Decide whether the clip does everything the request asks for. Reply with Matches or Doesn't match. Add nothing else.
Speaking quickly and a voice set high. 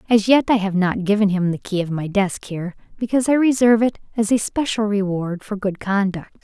Matches